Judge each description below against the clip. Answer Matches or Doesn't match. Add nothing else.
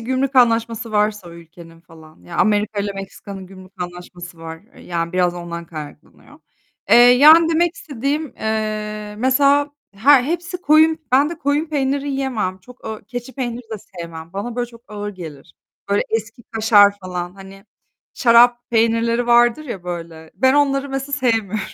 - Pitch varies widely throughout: Matches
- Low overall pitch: Doesn't match